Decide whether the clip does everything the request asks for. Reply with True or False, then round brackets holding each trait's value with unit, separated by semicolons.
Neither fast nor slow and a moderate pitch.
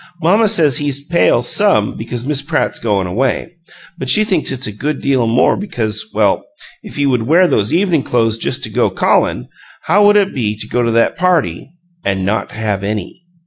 False (195 wpm; 130 Hz)